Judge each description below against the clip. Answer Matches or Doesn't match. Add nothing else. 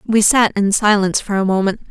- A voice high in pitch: Matches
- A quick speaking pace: Matches